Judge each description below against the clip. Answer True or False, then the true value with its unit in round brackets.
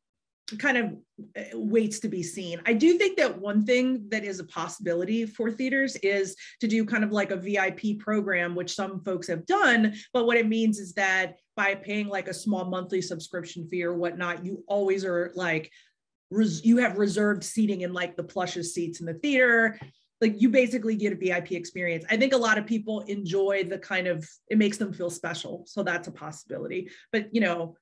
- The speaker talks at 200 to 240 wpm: True (205 wpm)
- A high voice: True (195 Hz)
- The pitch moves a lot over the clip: False (3.7 semitones)